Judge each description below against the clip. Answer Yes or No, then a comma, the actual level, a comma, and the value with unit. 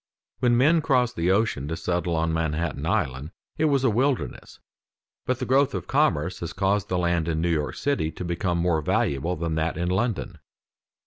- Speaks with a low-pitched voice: Yes, very low, 90 Hz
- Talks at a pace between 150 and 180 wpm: No, average, 190 wpm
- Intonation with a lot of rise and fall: Yes, wide, 6.9 semitones